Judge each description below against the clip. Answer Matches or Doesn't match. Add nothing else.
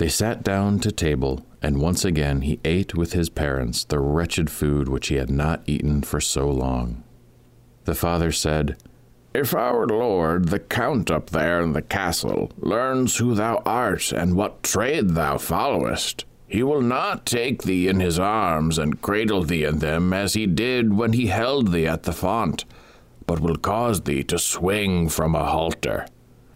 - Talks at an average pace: Matches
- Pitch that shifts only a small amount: Doesn't match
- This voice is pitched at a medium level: Doesn't match